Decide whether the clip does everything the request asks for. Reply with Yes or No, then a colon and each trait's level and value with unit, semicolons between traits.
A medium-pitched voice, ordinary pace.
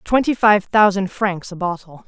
No: high, 195 Hz; average, 175 wpm